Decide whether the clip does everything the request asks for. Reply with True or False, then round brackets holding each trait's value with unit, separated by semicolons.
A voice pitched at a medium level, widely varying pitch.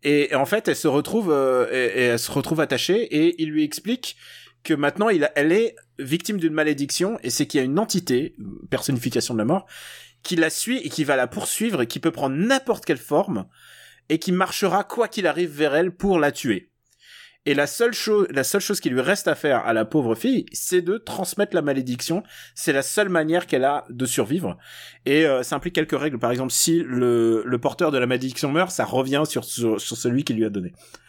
True (155 Hz; 6.2 semitones)